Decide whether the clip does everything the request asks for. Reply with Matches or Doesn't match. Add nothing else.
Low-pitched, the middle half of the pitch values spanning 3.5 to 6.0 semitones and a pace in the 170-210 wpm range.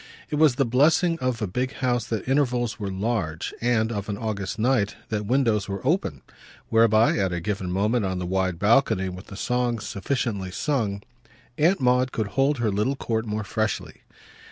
Matches